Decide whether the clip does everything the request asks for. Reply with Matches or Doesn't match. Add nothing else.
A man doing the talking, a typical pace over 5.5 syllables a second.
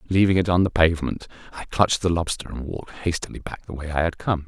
Matches